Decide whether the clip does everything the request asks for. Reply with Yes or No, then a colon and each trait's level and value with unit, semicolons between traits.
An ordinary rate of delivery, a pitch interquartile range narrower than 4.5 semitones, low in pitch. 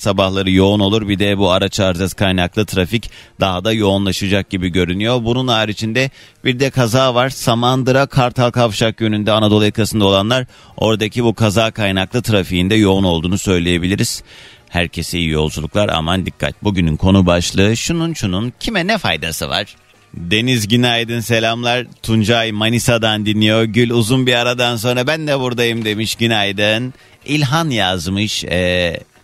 No: fast, 145 wpm; average, 3.9 semitones; low, 110 Hz